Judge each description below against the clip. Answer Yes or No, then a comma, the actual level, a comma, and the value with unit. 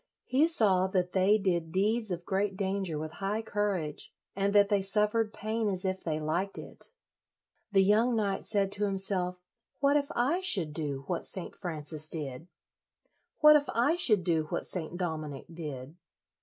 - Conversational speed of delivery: Yes, average, 170 wpm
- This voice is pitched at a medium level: No, high, 195 Hz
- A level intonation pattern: No, average, 4.1 semitones